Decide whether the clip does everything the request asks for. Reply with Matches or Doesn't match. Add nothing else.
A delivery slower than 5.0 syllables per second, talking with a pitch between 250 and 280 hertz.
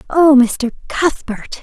Matches